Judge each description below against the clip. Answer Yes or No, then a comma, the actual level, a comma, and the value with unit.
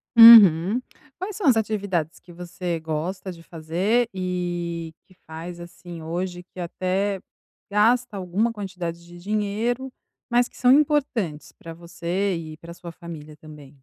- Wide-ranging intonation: No, average, 3.8 semitones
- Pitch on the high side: No, medium, 180 Hz